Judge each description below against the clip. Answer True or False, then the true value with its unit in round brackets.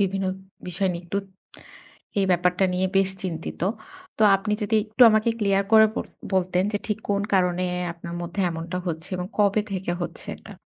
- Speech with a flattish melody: True (2.2 semitones)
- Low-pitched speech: False (190 Hz)